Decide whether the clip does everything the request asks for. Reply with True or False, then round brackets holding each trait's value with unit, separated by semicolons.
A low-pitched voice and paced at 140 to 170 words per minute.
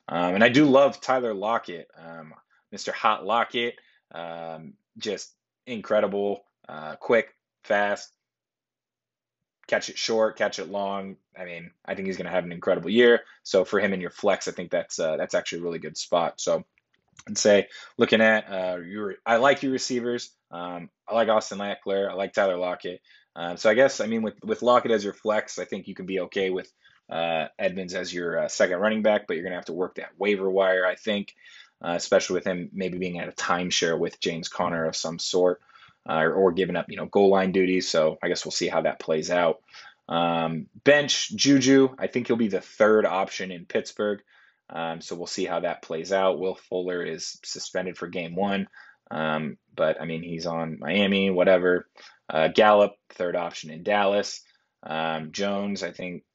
False (95 Hz; 200 wpm)